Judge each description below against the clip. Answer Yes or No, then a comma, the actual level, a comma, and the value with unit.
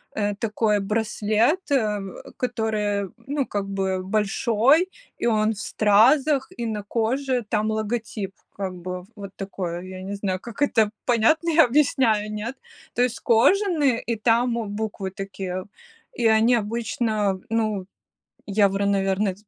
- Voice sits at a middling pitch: No, high, 215 Hz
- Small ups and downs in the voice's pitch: No, average, 3.1 semitones